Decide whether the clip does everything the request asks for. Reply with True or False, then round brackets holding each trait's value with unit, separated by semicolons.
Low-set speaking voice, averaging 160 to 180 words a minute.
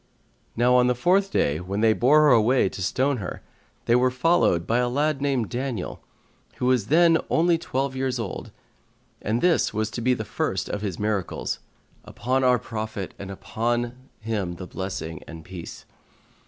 True (120 Hz; 175 wpm)